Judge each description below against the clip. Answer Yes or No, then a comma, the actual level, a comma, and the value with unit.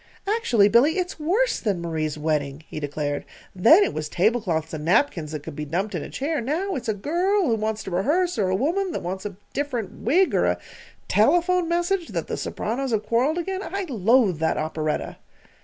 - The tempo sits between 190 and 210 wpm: Yes, average, 200 wpm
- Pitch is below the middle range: No, high, 230 Hz